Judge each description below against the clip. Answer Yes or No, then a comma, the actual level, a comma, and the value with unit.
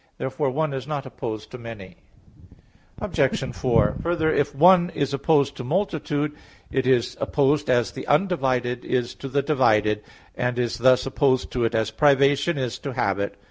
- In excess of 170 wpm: No, average, 165 wpm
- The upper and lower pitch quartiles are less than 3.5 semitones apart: Yes, average, 3.1 semitones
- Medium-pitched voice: No, low, 130 Hz